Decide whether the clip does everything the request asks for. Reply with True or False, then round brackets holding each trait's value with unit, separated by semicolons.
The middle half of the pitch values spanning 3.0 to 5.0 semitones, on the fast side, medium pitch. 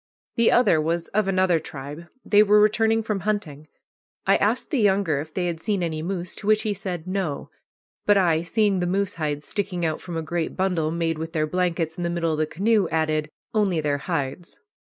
True (4.0 semitones; 210 wpm; 175 Hz)